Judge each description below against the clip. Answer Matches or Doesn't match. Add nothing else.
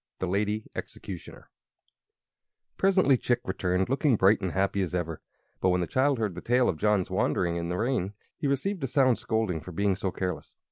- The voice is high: Doesn't match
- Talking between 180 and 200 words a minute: Matches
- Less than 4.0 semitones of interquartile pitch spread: Doesn't match